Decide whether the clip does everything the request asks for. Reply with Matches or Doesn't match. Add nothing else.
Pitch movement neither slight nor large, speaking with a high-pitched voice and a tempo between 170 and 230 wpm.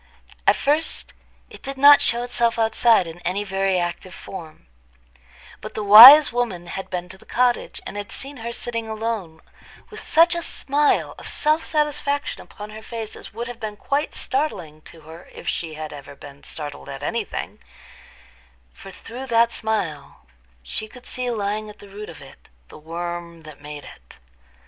Doesn't match